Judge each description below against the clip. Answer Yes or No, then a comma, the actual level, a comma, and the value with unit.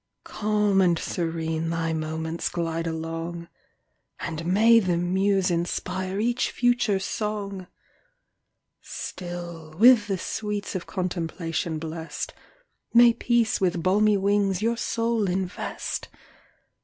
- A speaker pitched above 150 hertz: Yes, medium, 185 Hz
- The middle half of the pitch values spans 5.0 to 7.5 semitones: No, average, 3.9 semitones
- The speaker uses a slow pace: Yes, slow, 105 wpm